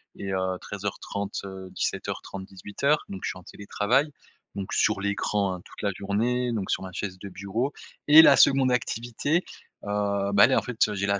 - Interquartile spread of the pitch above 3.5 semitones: Yes, average, 3.9 semitones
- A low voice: Yes, low, 100 Hz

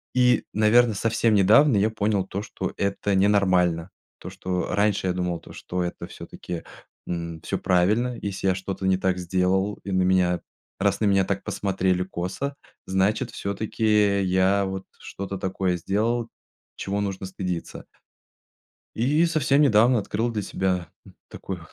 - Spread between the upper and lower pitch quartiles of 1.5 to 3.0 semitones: Yes, narrow, 2.6 semitones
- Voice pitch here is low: Yes, very low, 95 Hz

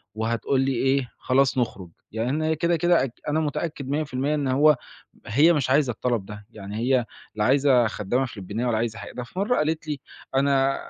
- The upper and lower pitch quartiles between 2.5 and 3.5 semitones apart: No, average, 4.0 semitones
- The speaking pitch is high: No, low, 135 Hz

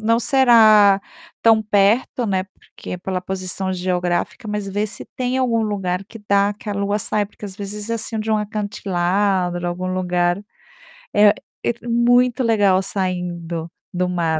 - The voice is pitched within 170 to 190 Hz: No, high, 200 Hz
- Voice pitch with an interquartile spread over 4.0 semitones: No, average, 3.0 semitones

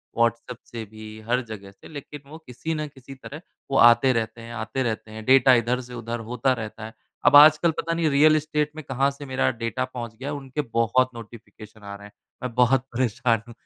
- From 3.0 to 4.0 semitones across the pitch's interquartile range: Yes, average, 3.3 semitones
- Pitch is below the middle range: Yes, low, 125 Hz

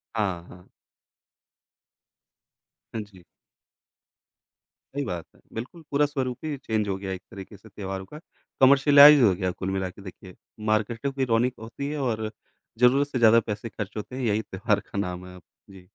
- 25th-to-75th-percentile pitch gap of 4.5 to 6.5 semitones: Yes, average, 5.3 semitones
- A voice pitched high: No, low, 110 Hz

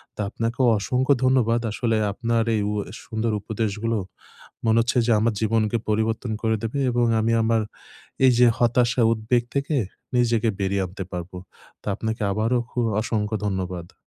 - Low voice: Yes, low, 115 Hz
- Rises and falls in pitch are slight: Yes, narrow, 2.0 semitones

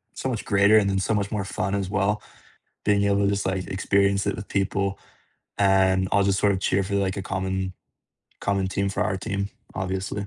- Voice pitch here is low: Yes, low, 100 Hz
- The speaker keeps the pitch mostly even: Yes, narrow, 1.0 semitones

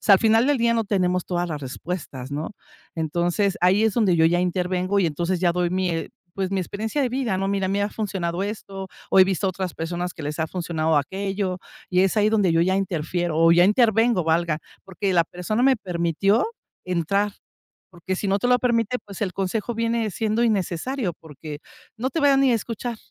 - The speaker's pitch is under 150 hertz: No, high, 190 Hz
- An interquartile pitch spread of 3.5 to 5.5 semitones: Yes, average, 3.8 semitones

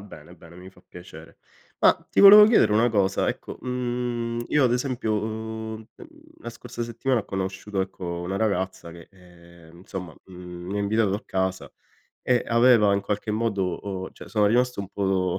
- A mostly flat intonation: No, average, 4.1 semitones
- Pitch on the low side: Yes, low, 100 Hz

